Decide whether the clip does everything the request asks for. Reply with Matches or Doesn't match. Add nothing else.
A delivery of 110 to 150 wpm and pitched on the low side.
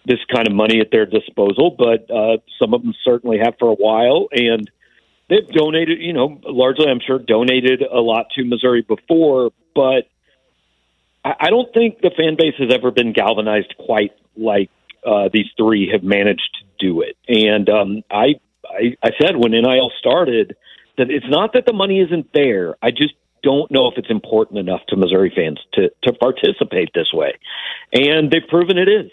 Doesn't match